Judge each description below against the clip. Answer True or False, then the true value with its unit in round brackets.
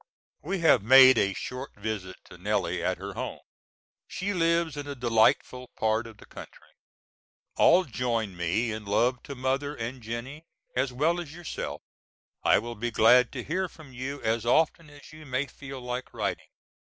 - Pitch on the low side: True (125 Hz)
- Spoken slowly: False (175 wpm)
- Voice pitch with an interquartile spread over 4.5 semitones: False (4.2 semitones)